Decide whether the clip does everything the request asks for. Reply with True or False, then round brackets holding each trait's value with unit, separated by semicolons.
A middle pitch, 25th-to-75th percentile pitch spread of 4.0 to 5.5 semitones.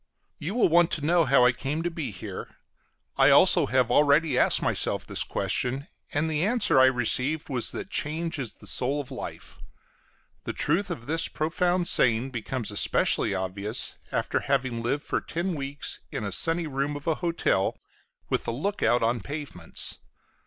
True (145 Hz; 4.9 semitones)